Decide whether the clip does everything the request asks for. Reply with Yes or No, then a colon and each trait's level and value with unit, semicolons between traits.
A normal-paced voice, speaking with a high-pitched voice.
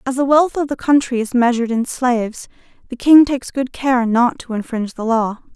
No: fast, 215 wpm; very high, 250 Hz